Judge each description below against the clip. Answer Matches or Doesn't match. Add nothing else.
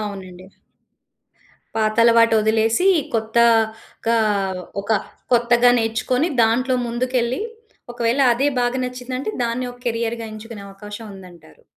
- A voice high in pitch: Matches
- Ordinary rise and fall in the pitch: Doesn't match